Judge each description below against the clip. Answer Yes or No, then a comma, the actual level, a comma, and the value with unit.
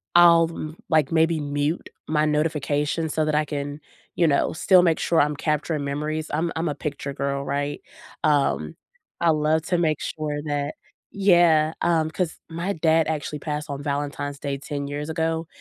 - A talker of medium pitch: Yes, medium, 155 Hz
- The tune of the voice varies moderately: No, narrow, 2.0 semitones